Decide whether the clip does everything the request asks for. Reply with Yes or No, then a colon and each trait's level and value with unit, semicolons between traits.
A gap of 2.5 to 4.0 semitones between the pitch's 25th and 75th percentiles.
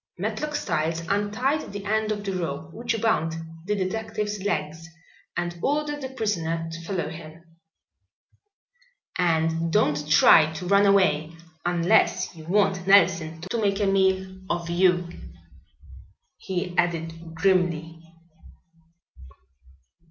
Yes: average, 3.7 semitones